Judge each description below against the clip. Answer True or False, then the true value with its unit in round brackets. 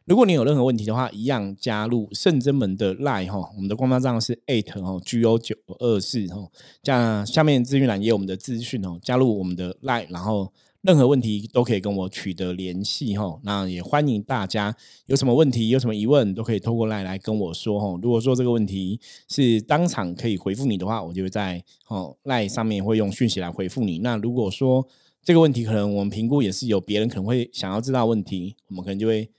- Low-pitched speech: True (110 Hz)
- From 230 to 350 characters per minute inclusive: False (370 characters per minute)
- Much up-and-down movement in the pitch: False (4.2 semitones)